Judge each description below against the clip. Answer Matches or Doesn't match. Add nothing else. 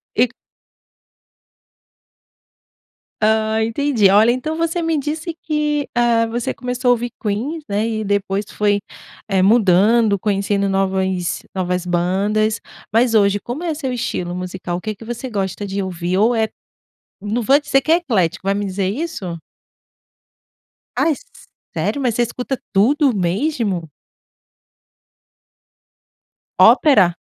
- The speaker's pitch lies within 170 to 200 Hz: Doesn't match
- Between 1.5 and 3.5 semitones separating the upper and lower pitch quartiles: Doesn't match